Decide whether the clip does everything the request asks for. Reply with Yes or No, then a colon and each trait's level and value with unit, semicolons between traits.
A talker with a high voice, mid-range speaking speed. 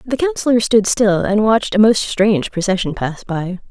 Yes: high, 210 Hz; average, 195 wpm